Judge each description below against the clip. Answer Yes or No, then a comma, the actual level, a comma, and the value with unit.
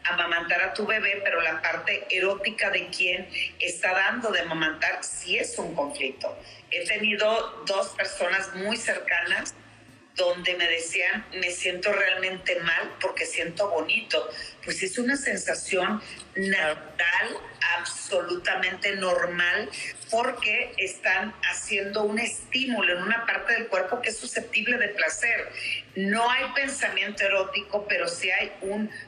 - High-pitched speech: Yes, high, 195 Hz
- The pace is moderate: Yes, average, 135 wpm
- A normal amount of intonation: Yes, average, 3.5 semitones